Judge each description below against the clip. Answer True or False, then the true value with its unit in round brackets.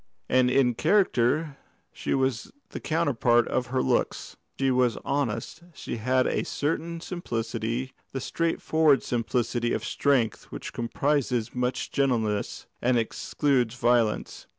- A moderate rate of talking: False (125 wpm)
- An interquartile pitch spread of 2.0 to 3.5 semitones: True (3.0 semitones)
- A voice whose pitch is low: True (125 Hz)